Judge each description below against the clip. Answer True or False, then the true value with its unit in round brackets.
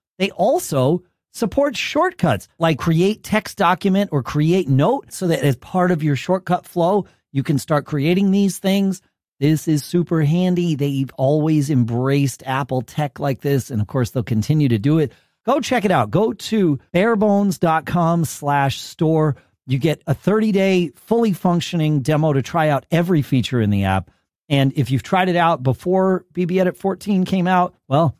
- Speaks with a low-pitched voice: False (165 Hz)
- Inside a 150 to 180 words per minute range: True (175 wpm)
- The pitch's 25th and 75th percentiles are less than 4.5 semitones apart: False (4.8 semitones)